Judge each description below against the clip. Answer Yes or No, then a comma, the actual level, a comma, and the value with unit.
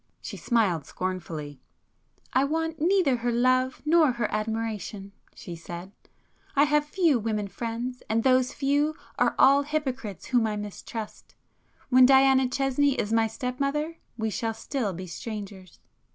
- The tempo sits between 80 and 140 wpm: Yes, slow, 135 wpm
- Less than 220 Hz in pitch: No, high, 245 Hz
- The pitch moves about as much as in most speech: Yes, average, 4.8 semitones